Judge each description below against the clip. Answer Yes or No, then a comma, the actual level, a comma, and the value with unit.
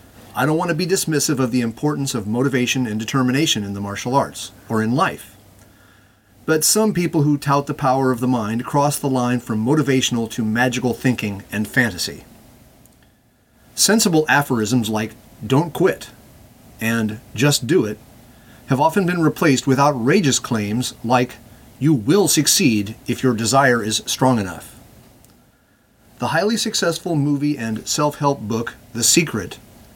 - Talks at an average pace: Yes, average, 150 wpm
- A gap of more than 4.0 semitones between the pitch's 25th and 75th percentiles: Yes, average, 4.5 semitones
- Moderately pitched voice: No, low, 125 Hz